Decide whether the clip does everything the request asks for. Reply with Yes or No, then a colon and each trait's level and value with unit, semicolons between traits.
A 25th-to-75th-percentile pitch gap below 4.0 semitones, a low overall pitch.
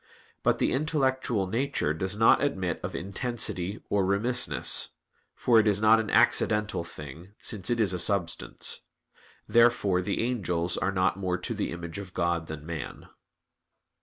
No: average, 4.5 semitones; low, 100 Hz